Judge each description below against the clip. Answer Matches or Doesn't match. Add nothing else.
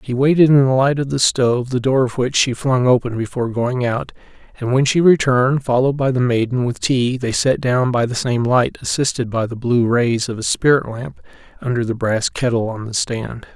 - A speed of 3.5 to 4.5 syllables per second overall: Doesn't match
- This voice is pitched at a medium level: Doesn't match